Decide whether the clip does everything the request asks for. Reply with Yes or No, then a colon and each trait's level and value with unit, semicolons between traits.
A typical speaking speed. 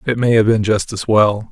No: fast, 275 wpm